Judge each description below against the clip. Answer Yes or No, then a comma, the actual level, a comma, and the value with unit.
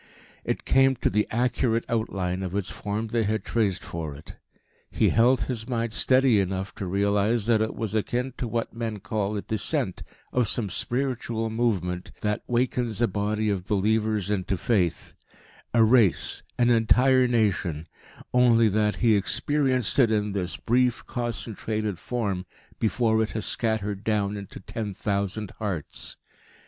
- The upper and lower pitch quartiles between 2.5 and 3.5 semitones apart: Yes, average, 2.9 semitones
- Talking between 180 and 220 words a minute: No, average, 155 wpm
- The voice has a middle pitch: No, low, 110 Hz